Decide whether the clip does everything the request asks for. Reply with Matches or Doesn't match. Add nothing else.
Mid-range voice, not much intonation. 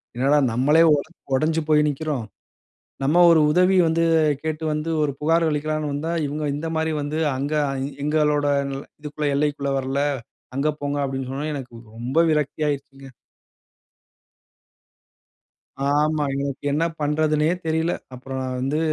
Matches